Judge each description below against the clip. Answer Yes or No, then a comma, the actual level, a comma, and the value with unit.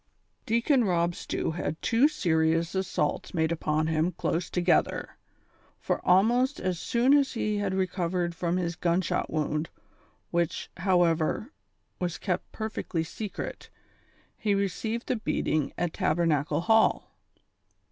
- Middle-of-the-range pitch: Yes, medium, 180 Hz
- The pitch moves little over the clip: No, average, 4.4 semitones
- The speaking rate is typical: No, slow, 125 wpm